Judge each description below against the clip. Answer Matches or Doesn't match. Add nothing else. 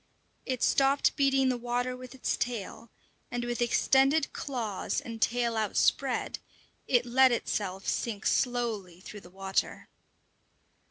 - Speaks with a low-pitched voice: Doesn't match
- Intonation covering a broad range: Doesn't match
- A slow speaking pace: Matches